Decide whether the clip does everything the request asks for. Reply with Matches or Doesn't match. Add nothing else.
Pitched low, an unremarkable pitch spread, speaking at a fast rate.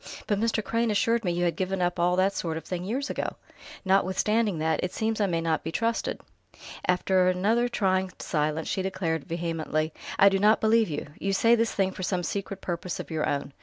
Doesn't match